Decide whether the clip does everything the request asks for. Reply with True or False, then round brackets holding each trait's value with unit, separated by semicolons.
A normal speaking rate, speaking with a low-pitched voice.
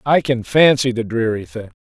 True (195 wpm; 130 Hz)